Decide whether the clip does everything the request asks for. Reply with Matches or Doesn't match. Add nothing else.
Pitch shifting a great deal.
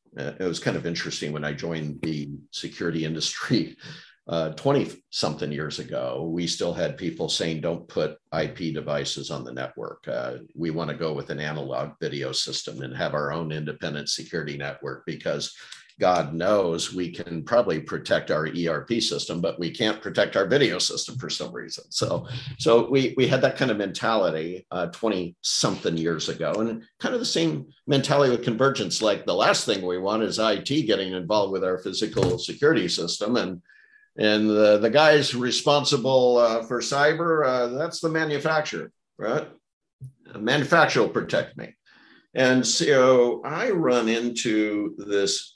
Matches